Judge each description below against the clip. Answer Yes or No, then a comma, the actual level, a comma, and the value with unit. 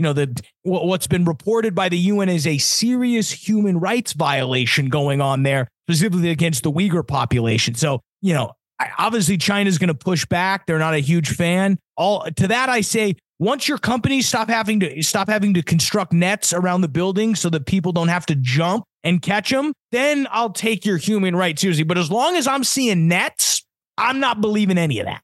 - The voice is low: No, medium, 185 Hz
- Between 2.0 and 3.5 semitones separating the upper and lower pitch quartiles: No, average, 4.7 semitones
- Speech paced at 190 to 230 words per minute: Yes, fast, 205 wpm